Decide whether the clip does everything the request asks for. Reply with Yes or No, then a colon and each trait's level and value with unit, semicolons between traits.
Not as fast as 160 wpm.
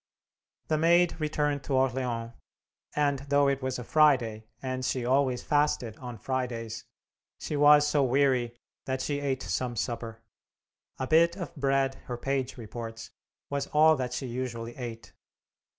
Yes: average, 150 wpm